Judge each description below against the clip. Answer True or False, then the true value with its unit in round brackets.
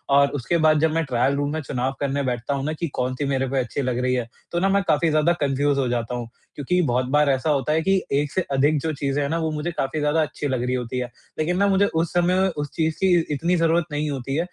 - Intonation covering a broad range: False (3.3 semitones)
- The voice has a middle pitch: True (145 Hz)